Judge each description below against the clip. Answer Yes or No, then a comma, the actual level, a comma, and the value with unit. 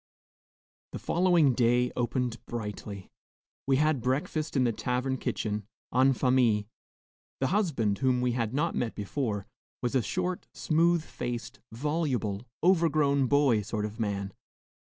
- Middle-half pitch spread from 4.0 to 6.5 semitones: Yes, average, 4.7 semitones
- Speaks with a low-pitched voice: Yes, low, 125 Hz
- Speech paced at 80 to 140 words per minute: Yes, slow, 135 wpm